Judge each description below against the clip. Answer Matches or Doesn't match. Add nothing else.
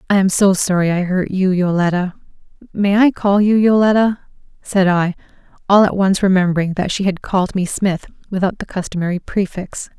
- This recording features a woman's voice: Matches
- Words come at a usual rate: Matches